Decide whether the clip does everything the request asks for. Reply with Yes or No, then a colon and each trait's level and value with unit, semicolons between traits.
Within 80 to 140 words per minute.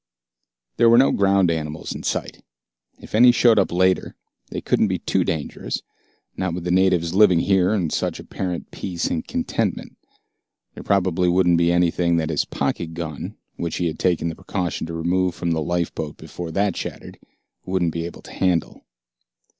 No: average, 175 wpm